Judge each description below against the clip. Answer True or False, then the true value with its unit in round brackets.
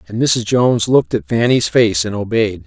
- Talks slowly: False (200 wpm)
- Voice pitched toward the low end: True (115 Hz)